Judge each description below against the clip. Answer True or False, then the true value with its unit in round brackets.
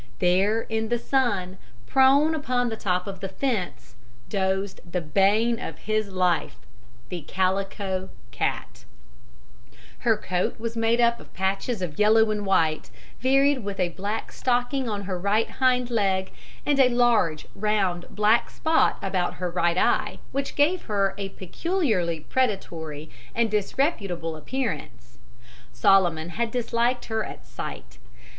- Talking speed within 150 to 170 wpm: False (140 wpm)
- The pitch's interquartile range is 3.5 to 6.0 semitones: True (4.7 semitones)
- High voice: True (200 Hz)